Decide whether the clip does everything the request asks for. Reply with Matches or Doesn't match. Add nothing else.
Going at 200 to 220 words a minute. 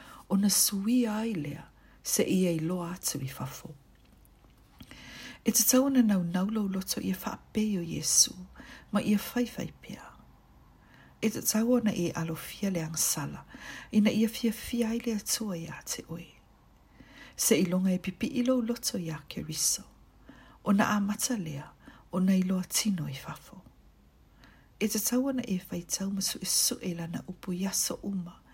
Doesn't match